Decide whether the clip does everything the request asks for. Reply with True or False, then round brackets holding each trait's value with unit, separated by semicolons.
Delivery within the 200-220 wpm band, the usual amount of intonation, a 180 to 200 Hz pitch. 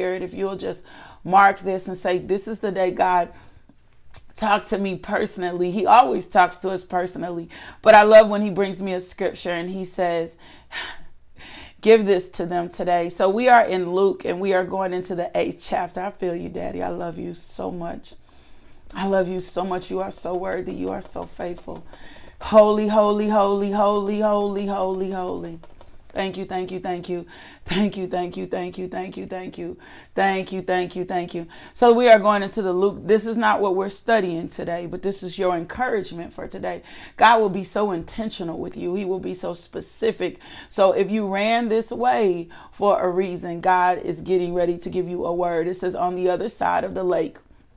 False (205 wpm; 2.2 semitones; 185 Hz)